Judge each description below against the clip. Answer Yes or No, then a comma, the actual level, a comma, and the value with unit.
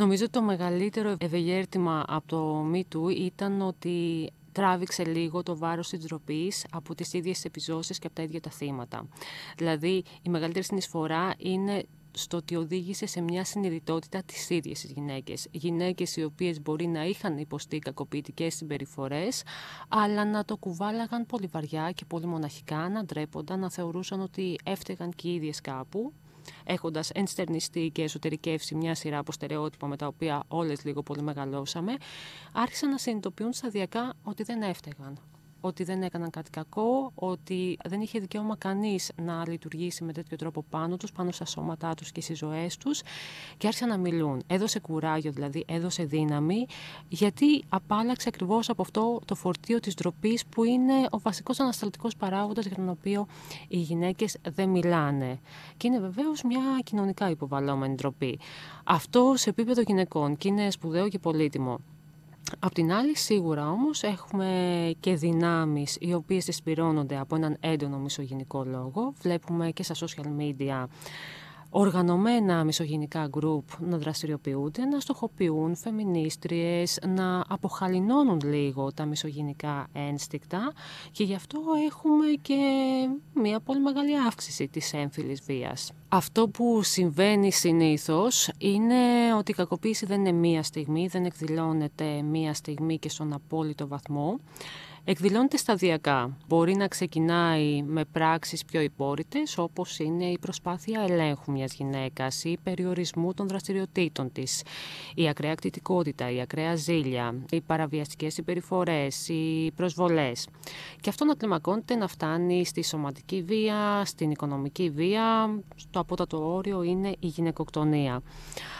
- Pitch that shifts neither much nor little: Yes, average, 3.9 semitones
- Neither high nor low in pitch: Yes, medium, 170 Hz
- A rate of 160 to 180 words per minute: No, average, 140 wpm